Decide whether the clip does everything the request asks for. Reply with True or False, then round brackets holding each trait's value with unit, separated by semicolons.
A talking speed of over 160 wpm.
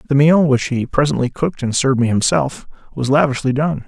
True (200 wpm)